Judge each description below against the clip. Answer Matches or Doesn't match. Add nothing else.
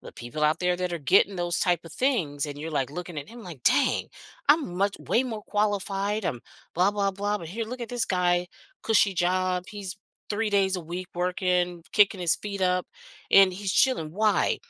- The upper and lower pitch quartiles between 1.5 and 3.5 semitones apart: Matches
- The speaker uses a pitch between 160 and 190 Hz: Matches